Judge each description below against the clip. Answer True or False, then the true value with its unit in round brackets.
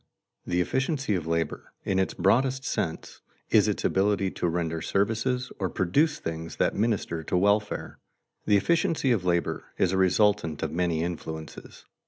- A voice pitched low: True (95 Hz)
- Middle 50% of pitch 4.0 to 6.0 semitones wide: True (4.6 semitones)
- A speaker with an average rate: True (155 wpm)